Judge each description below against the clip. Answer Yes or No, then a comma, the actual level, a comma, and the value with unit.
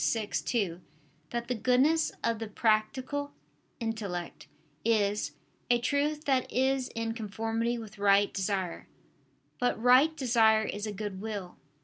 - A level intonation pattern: No, average, 3.3 semitones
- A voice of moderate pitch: No, high, 225 Hz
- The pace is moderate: No, slow, 130 wpm